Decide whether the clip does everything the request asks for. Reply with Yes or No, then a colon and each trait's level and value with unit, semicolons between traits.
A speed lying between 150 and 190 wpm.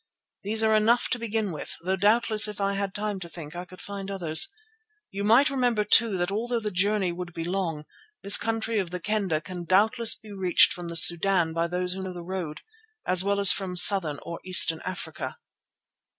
No: fast, 205 wpm